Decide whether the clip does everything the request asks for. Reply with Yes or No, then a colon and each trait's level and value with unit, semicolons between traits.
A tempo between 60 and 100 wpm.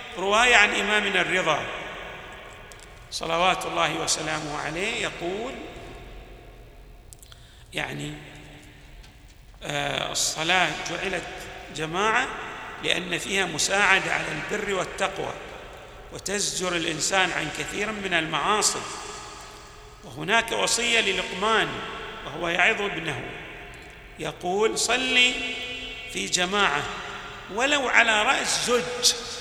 Yes: average, 80 wpm